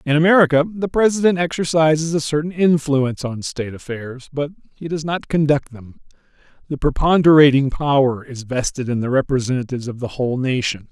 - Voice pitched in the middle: Yes, medium, 145 Hz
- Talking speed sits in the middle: Yes, average, 160 wpm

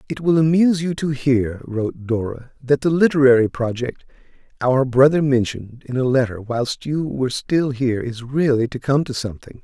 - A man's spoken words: Yes, male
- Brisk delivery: No, average, 180 wpm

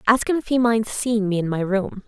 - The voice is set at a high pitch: Yes, high, 220 Hz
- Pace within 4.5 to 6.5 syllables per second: Yes, 5.2 syllables/s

